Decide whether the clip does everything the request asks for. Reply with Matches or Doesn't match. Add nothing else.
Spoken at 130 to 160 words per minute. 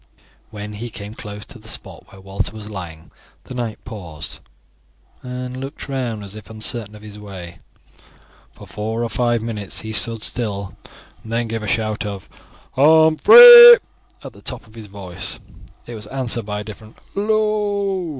Doesn't match